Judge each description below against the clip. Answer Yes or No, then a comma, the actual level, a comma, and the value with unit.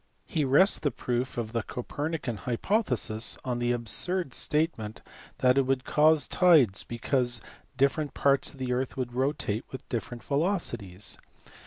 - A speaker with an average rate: Yes, average, 145 wpm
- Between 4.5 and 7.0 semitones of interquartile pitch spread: No, average, 3.8 semitones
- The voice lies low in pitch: Yes, low, 130 Hz